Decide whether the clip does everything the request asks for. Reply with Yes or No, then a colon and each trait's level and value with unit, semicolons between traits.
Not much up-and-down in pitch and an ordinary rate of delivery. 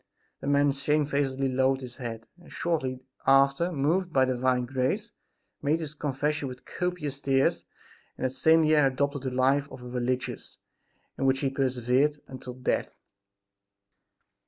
Yes: narrow, 2.3 semitones; average, 145 wpm